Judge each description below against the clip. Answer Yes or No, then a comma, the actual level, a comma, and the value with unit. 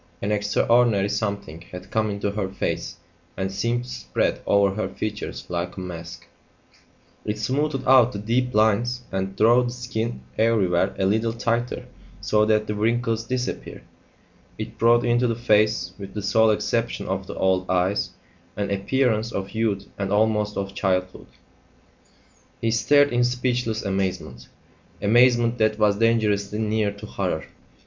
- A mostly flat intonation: No, average, 3.0 semitones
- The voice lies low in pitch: Yes, low, 105 Hz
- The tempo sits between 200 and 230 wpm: No, average, 150 wpm